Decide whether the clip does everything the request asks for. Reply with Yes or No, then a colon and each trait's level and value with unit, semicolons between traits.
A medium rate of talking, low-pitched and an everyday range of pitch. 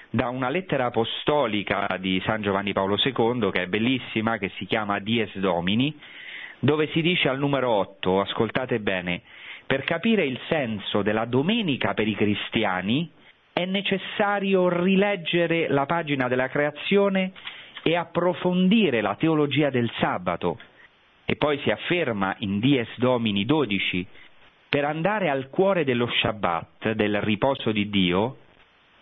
No: average, 135 wpm; low, 125 Hz; wide, 7.7 semitones